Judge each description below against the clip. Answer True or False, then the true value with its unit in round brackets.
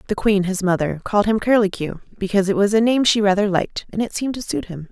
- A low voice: False (200 Hz)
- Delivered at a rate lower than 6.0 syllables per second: False (6.7 syllables/s)